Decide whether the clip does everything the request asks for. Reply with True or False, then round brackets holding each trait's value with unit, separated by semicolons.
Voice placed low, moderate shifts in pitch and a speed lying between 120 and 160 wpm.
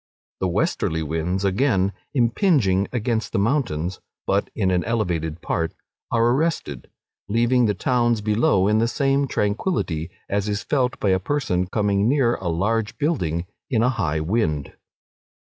True (105 Hz; 4.8 semitones; 145 wpm)